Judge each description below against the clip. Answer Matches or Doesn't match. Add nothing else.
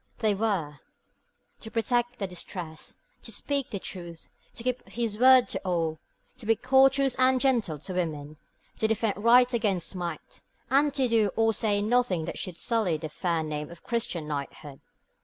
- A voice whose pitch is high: Matches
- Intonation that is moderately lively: Doesn't match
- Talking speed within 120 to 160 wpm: Doesn't match